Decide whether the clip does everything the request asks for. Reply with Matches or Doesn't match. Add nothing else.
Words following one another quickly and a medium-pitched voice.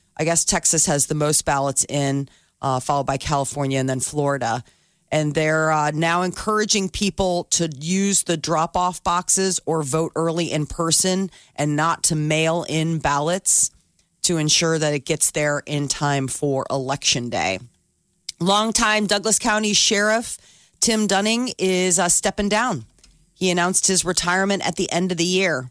Doesn't match